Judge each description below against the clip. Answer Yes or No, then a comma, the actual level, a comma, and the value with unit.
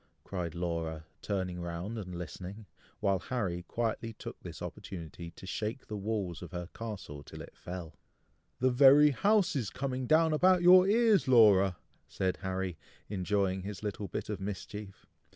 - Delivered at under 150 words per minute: No, average, 155 wpm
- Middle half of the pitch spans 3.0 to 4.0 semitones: No, wide, 5.6 semitones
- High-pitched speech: No, low, 100 Hz